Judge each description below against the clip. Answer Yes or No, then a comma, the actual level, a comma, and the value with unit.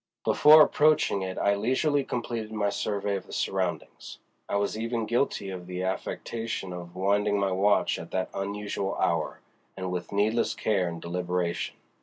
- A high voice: No, low, 100 Hz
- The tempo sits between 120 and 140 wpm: No, average, 160 wpm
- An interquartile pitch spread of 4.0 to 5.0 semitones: No, average, 3.1 semitones